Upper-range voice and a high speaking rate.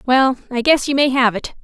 Yes: very high, 260 Hz; fast, 260 wpm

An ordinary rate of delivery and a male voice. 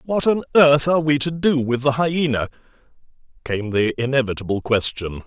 Yes: average, 160 wpm; male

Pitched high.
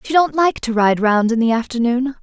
Yes: very high, 250 Hz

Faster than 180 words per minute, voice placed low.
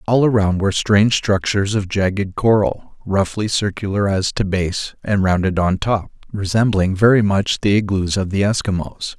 No: average, 165 wpm; low, 100 Hz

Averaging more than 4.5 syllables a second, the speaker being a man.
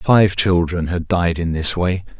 No: 3.9 syllables/s; male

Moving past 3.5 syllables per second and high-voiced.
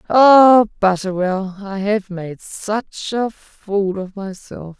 No: 2.9 syllables/s; high, 200 Hz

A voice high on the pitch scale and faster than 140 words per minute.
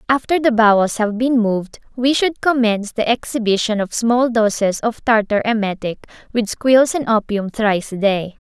Yes: high, 225 Hz; average, 170 wpm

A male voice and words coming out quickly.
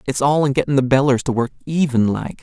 Yes: male; fast, 245 wpm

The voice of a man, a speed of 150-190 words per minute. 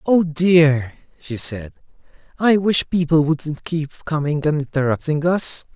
No: male; slow, 135 wpm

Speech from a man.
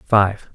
Yes: male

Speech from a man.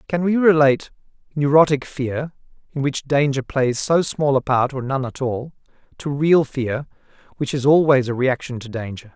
Yes: male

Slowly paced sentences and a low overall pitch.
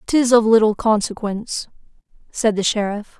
No: slow, 130 wpm; high, 215 Hz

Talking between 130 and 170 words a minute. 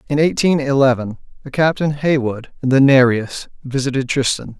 Yes: average, 145 wpm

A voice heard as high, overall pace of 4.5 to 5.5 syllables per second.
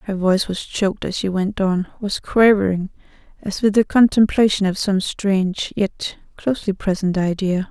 Yes: high, 195 Hz; 4.9 syllables/s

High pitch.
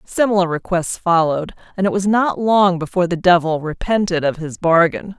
No: medium, 180 Hz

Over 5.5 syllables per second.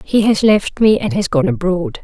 No: 4.7 syllables/s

